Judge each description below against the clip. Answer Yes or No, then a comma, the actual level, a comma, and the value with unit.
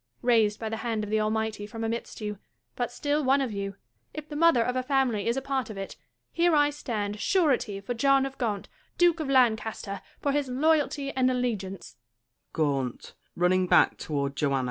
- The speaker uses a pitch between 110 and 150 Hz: No, high, 245 Hz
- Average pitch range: Yes, average, 4.5 semitones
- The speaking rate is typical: Yes, average, 175 wpm